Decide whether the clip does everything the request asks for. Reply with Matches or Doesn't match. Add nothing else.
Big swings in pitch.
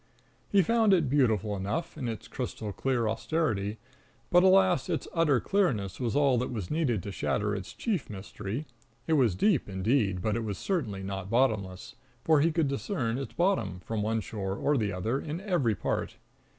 Matches